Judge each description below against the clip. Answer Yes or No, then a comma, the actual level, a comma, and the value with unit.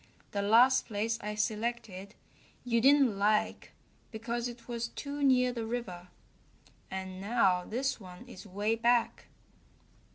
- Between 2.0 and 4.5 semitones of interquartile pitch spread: Yes, average, 3.2 semitones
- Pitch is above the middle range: Yes, high, 225 Hz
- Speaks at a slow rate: Yes, slow, 130 wpm